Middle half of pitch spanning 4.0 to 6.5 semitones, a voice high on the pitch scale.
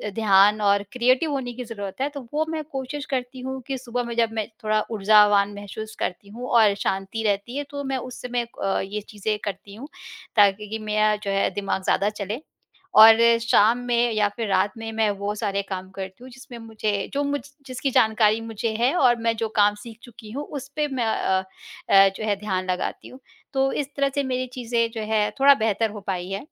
No: average, 3.5 semitones; high, 220 Hz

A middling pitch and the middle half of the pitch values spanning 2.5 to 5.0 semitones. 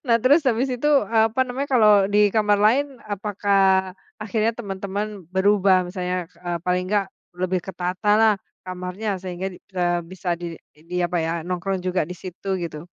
No: high, 195 Hz; average, 2.9 semitones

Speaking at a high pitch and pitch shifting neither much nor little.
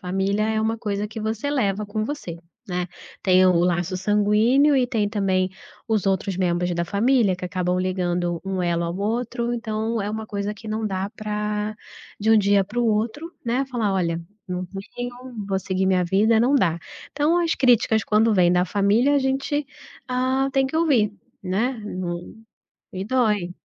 Yes: high, 210 Hz; average, 4.1 semitones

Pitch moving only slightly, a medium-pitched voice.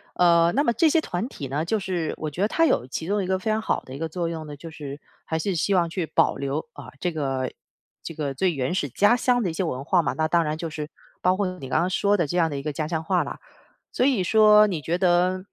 No: average, 4.0 semitones; medium, 170 Hz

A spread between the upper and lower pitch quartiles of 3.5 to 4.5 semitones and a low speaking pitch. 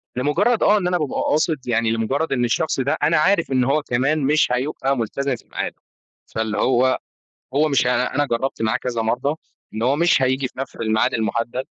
Yes: average, 3.8 semitones; low, 130 Hz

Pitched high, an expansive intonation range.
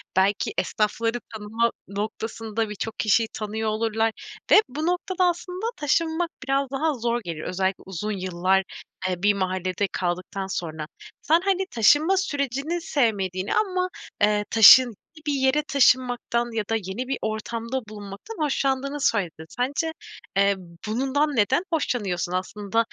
Yes: high, 225 Hz; wide, 5.8 semitones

